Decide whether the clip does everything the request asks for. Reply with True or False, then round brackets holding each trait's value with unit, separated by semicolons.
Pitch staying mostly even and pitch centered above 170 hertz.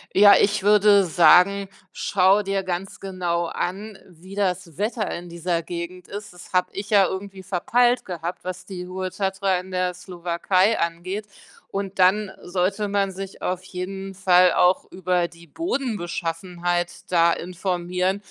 True (1.9 semitones; 185 Hz)